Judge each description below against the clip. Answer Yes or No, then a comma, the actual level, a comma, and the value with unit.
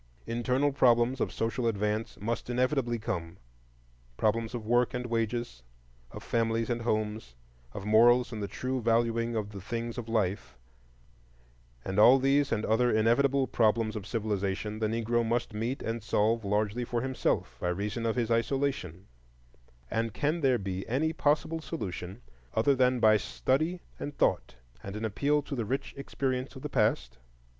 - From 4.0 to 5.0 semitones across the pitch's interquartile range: No, average, 3.0 semitones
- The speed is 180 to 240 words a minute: No, average, 160 wpm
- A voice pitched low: Yes, low, 115 Hz